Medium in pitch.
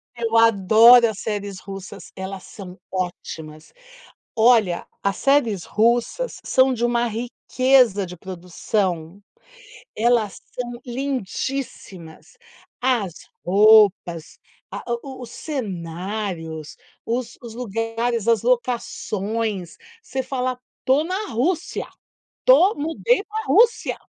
No: high, 225 Hz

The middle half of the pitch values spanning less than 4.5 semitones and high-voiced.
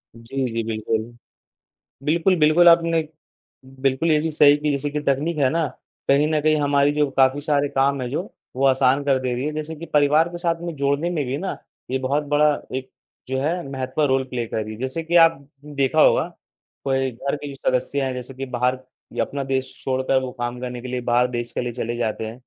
No: average, 2.8 semitones; medium, 140 Hz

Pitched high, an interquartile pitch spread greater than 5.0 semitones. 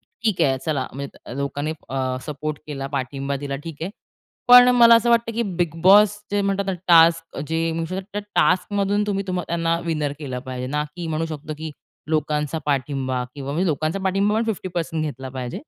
No: medium, 160 Hz; wide, 5.4 semitones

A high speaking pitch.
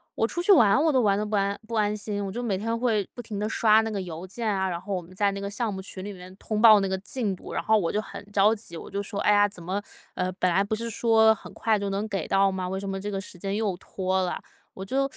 Yes: high, 200 Hz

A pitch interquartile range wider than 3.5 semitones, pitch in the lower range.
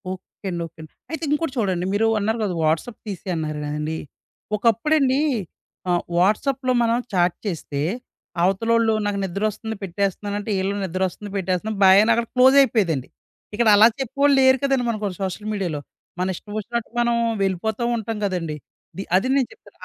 No: average, 4.1 semitones; high, 205 Hz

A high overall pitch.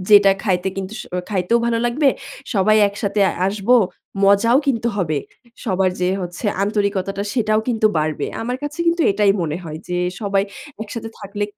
Yes: high, 200 Hz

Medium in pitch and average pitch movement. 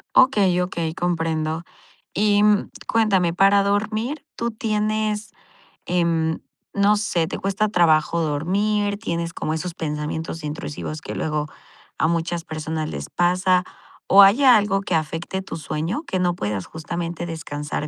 Yes: medium, 175 Hz; average, 4.2 semitones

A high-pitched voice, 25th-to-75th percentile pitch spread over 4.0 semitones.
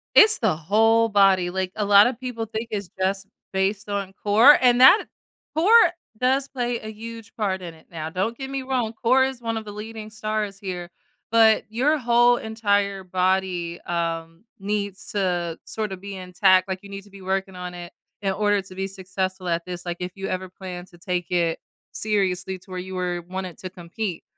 No: high, 195 Hz; average, 3.4 semitones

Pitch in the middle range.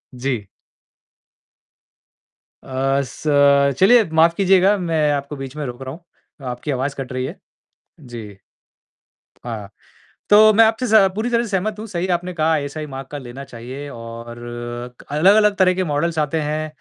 Yes: medium, 150 Hz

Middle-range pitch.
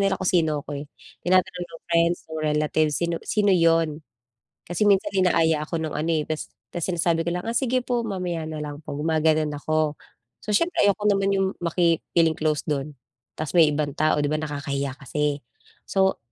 Yes: medium, 160 Hz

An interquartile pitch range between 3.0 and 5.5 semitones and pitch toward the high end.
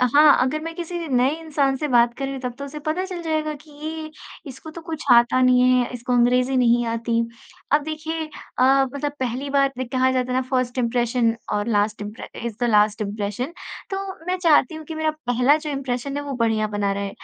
Yes: average, 4.2 semitones; very high, 260 Hz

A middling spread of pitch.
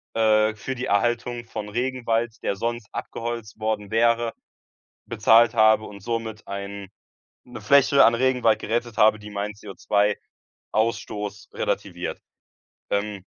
No: narrow, 2.0 semitones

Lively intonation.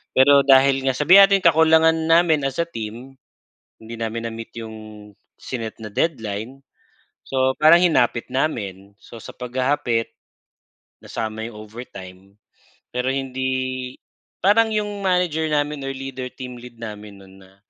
No: average, 4.8 semitones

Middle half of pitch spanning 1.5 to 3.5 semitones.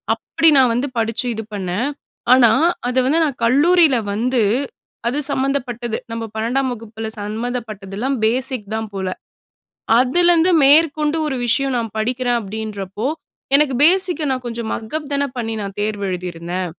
No: average, 4.0 semitones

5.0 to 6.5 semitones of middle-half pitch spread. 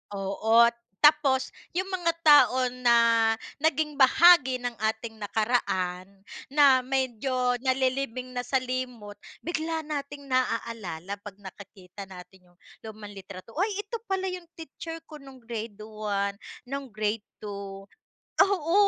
Yes: wide, 5.5 semitones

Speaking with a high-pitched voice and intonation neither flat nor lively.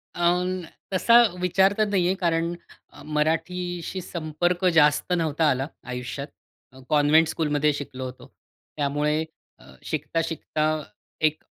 No: medium, 160 Hz; average, 3.1 semitones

